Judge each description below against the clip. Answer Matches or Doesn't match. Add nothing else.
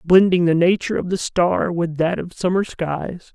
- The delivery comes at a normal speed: Matches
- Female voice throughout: Doesn't match